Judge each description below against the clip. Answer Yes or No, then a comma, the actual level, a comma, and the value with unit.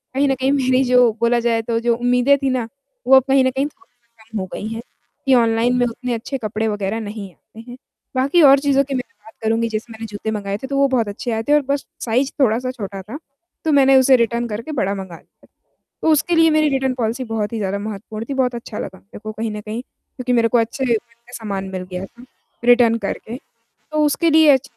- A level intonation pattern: No, average, 3.2 semitones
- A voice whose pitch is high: Yes, high, 235 Hz